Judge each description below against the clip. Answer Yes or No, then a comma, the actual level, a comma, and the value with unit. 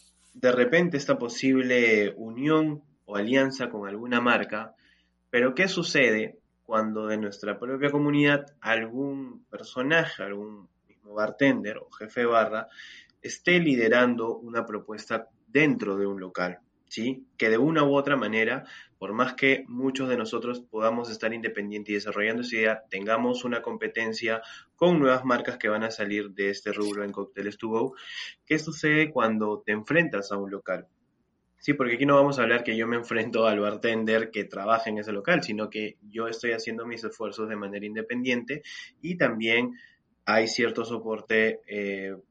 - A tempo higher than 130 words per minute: Yes, average, 160 wpm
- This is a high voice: No, low, 115 Hz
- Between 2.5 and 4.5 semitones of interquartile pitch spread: Yes, average, 3.4 semitones